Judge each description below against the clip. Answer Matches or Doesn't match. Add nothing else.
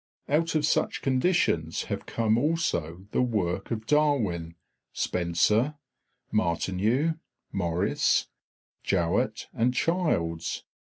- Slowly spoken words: Matches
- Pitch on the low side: Matches